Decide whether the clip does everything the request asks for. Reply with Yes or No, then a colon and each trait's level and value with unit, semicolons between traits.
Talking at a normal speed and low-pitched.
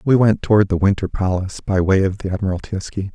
No: fast, 210 wpm; very low, 95 Hz